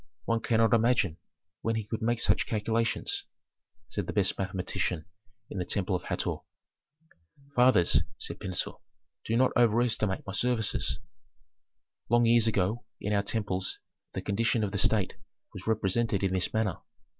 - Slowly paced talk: No, average, 145 wpm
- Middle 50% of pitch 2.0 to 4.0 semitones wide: Yes, average, 3.1 semitones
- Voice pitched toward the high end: No, low, 110 Hz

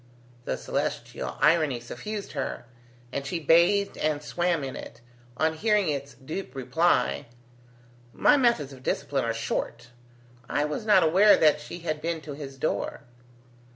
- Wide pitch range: No, average, 4.2 semitones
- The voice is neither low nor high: Yes, medium, 155 Hz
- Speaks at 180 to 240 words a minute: No, average, 150 wpm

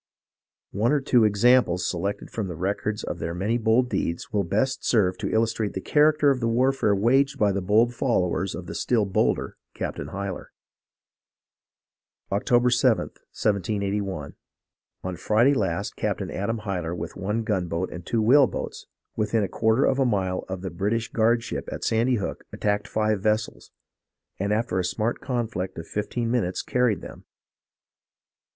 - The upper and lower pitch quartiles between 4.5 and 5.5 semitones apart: No, average, 3.8 semitones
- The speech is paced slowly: No, average, 160 wpm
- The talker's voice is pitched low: Yes, low, 105 Hz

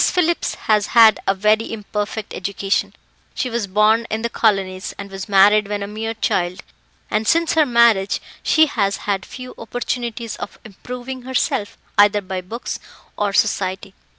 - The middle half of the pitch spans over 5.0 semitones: No, average, 2.9 semitones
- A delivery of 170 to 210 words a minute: No, average, 155 wpm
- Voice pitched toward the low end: No, high, 215 Hz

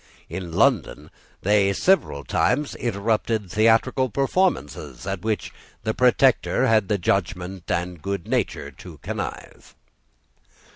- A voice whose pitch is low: Yes, low, 100 Hz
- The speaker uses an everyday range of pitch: Yes, average, 4.2 semitones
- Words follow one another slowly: Yes, slow, 110 wpm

